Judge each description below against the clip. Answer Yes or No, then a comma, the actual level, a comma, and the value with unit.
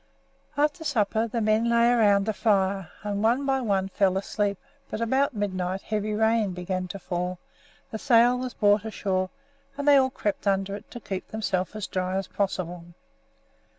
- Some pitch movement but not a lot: Yes, average, 3.3 semitones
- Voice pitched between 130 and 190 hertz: No, high, 205 Hz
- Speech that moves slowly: No, average, 175 wpm